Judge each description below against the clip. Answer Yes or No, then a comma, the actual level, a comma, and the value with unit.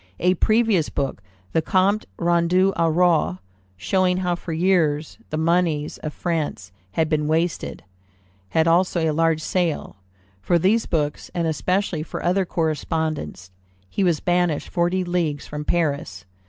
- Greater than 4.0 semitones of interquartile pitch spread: No, average, 2.7 semitones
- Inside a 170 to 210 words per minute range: No, average, 140 wpm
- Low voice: No, medium, 165 Hz